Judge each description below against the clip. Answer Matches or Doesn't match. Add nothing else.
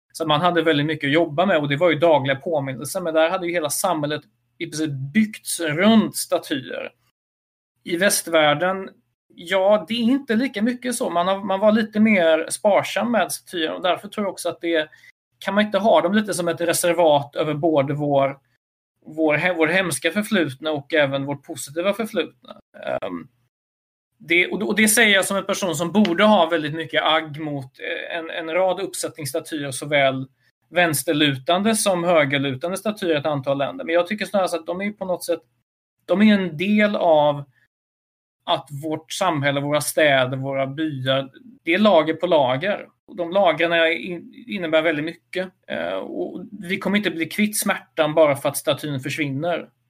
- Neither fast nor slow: Matches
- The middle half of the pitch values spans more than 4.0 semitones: Matches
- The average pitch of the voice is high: Doesn't match